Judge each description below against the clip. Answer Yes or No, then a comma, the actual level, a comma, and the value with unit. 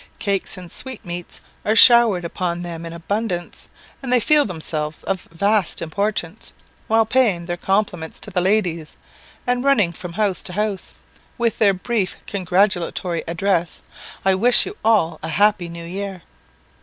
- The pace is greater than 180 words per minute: No, average, 150 wpm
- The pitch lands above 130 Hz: Yes, high, 190 Hz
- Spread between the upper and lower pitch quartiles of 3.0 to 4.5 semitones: Yes, average, 3.9 semitones